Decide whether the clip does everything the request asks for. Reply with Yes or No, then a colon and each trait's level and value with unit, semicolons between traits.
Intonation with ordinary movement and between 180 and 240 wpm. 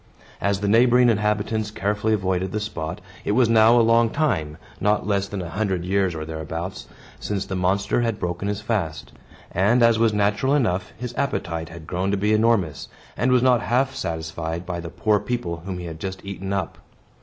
Yes: average, 3.9 semitones; average, 195 wpm